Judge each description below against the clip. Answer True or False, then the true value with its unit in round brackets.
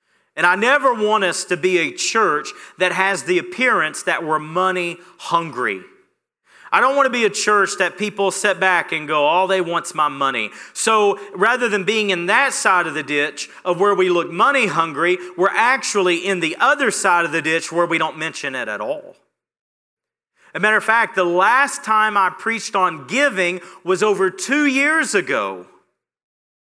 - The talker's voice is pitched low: False (185 Hz)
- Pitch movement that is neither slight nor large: True (3.7 semitones)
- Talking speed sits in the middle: True (190 wpm)